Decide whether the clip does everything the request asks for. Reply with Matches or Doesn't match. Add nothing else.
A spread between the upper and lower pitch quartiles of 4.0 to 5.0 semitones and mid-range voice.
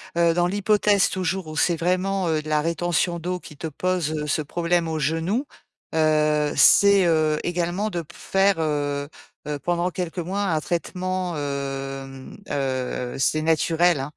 Doesn't match